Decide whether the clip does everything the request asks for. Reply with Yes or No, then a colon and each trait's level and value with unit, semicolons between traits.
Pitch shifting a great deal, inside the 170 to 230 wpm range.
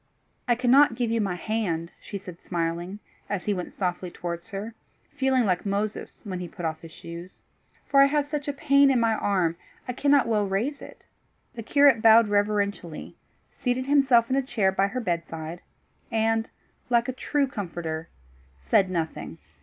Yes: wide, 6.0 semitones; average, 175 wpm